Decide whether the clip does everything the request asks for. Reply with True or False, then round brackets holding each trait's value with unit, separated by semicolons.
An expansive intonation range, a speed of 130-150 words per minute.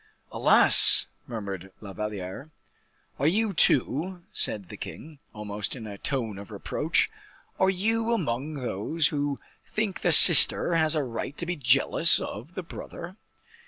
True (8.2 semitones; 145 wpm)